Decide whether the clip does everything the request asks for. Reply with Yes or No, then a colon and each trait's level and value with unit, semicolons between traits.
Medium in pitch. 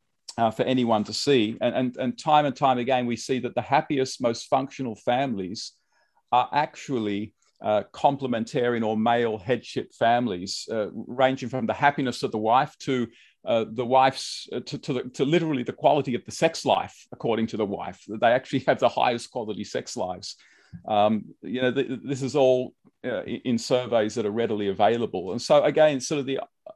No: low, 125 Hz